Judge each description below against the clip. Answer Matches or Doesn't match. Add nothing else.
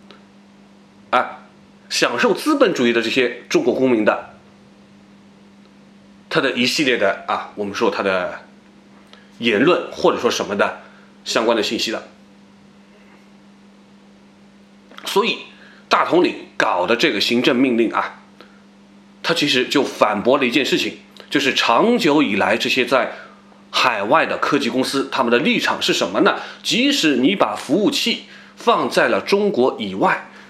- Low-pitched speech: Matches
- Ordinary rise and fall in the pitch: Matches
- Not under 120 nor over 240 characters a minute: Matches